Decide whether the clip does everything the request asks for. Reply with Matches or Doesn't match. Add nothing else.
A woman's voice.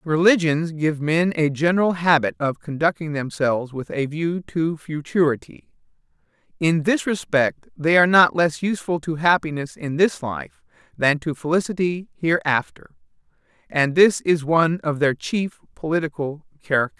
Doesn't match